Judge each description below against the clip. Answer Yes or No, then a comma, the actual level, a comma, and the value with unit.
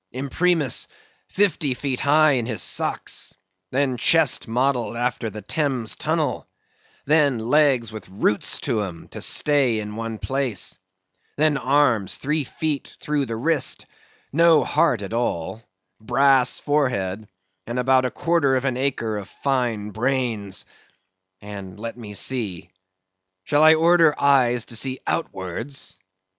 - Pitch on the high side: No, low, 125 Hz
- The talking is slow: Yes, slow, 130 wpm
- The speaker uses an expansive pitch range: No, average, 4.7 semitones